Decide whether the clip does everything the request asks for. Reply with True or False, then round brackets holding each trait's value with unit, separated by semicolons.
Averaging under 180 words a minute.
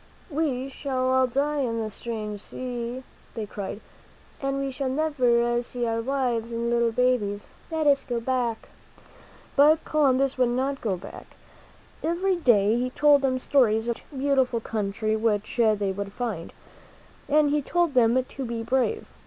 True (160 wpm)